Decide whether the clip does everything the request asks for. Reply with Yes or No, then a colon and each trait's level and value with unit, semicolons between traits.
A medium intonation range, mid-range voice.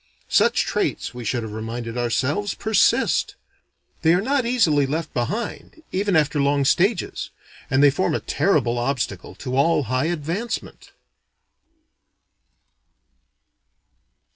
No: wide, 6.8 semitones; medium, 145 Hz